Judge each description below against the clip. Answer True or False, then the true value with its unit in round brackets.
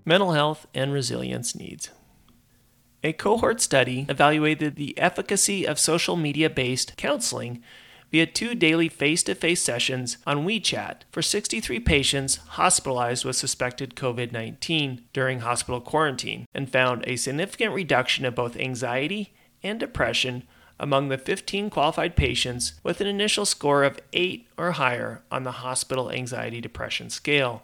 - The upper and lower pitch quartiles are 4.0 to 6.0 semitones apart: True (4.3 semitones)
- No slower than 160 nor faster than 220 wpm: False (140 wpm)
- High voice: False (135 Hz)